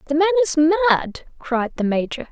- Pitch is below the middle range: No, very high, 305 Hz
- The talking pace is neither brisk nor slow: Yes, average, 180 wpm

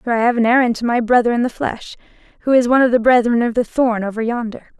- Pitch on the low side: No, high, 235 Hz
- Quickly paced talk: Yes, fast, 275 wpm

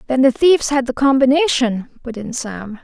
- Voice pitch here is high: Yes, very high, 255 Hz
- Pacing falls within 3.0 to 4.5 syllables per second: No, 5.0 syllables/s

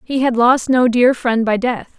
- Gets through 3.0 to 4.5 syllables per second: Yes, 4.2 syllables/s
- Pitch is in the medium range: No, high, 245 Hz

